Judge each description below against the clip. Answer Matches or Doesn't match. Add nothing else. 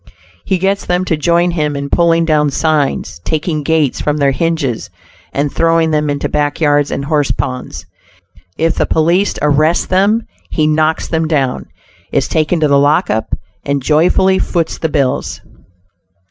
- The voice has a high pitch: Doesn't match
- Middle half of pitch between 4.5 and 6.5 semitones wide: Doesn't match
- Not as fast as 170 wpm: Matches